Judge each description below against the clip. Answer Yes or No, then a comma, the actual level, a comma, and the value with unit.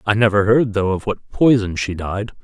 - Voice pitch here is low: Yes, low, 105 Hz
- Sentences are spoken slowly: No, fast, 220 wpm